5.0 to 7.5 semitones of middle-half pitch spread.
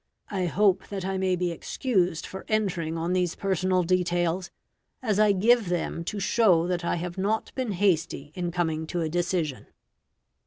No: narrow, 2.4 semitones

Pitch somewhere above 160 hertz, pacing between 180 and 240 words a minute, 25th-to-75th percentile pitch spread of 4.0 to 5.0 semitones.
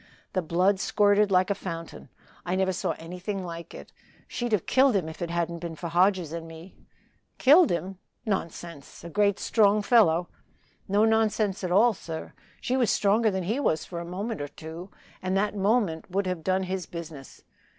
No: medium, 185 Hz; average, 185 wpm; average, 3.4 semitones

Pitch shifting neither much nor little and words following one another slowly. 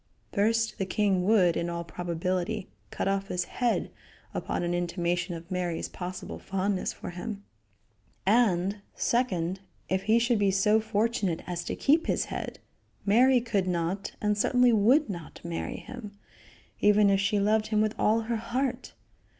No: average, 3.7 semitones; average, 160 wpm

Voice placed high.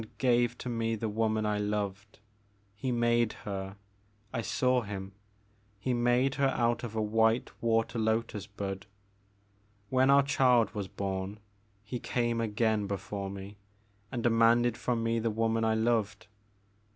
No: low, 110 Hz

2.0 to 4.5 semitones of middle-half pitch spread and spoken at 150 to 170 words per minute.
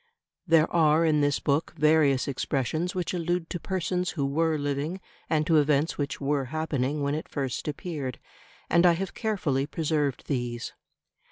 Yes: average, 2.8 semitones; average, 160 wpm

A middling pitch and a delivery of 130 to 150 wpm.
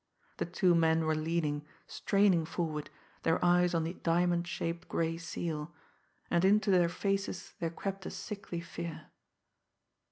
Yes: medium, 170 Hz; average, 140 wpm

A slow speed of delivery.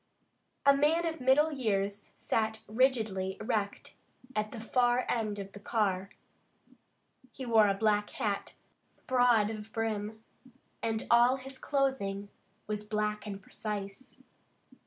Yes: slow, 125 wpm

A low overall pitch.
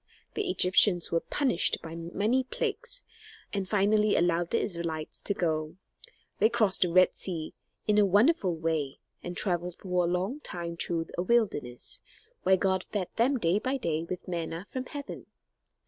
No: medium, 185 Hz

